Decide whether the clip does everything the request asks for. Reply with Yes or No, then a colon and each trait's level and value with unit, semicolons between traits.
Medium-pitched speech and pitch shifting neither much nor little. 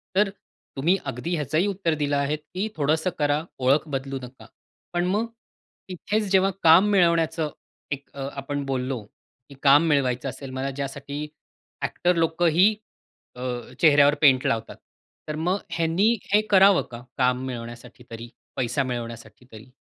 Yes: medium, 145 Hz; average, 4.7 semitones